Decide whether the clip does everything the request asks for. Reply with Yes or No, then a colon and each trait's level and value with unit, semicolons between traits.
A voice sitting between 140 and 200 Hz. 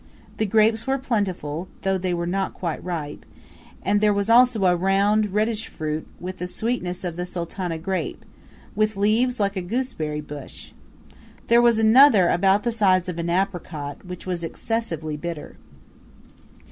Yes: high, 190 Hz